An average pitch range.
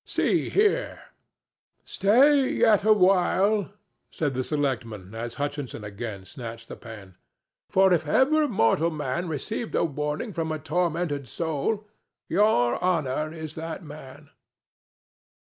No: wide, 6.7 semitones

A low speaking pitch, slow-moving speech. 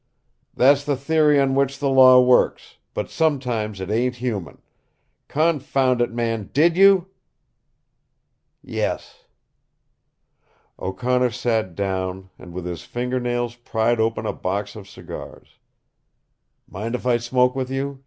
Yes: low, 125 Hz; slow, 130 wpm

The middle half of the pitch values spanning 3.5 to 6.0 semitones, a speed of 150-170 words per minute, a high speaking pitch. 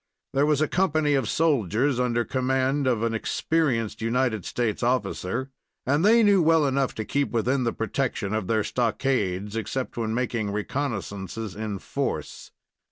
No: average, 4.2 semitones; average, 155 wpm; low, 125 Hz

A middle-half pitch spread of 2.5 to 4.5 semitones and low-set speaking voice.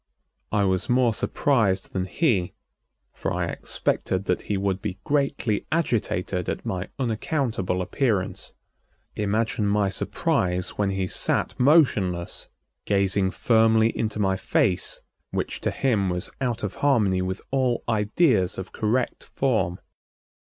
Yes: average, 4.2 semitones; low, 105 Hz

